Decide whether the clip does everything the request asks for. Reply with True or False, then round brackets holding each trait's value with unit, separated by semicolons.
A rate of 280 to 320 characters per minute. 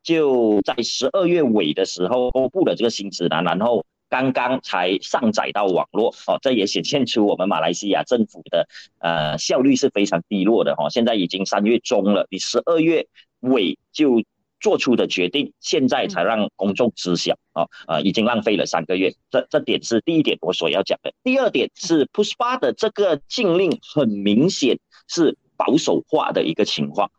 True (285 characters per minute)